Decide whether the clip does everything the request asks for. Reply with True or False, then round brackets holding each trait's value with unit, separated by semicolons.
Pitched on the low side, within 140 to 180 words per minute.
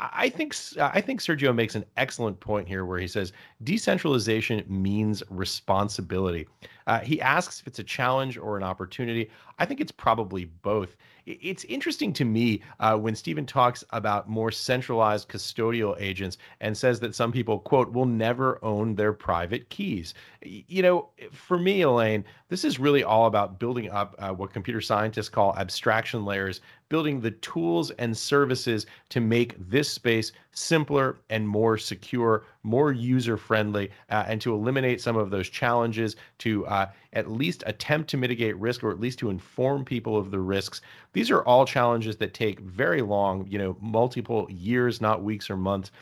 True (110 Hz; 170 wpm)